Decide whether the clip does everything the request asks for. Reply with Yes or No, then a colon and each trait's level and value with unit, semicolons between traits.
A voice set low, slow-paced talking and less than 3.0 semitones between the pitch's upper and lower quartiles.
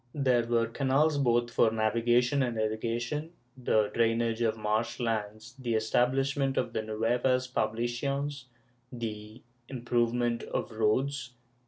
Yes: low, 120 Hz; slow, 120 wpm; narrow, 2.4 semitones